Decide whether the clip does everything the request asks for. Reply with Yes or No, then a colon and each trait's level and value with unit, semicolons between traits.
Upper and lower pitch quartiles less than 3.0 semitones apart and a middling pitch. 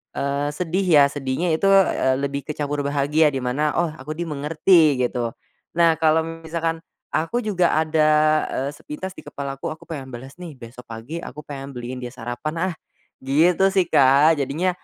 No: average, 3.3 semitones; medium, 150 Hz